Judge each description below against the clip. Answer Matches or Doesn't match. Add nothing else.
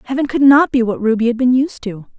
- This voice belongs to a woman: Matches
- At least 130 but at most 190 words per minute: Doesn't match